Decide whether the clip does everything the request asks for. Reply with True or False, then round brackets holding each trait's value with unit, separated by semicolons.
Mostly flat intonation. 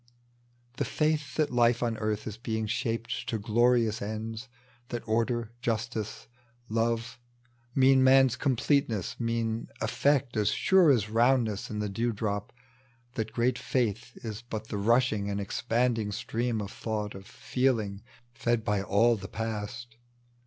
True (2.1 semitones)